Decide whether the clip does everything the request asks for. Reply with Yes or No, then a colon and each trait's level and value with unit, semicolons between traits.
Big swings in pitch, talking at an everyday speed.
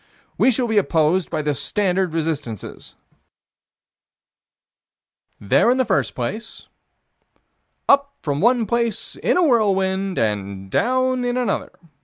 No: wide, 8.4 semitones; slow, 120 wpm